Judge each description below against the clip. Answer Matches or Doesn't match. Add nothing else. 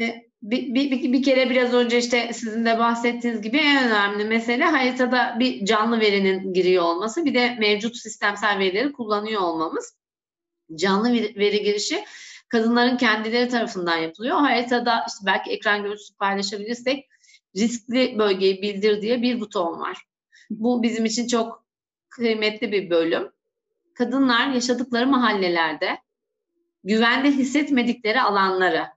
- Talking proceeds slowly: Doesn't match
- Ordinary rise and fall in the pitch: Matches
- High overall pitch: Matches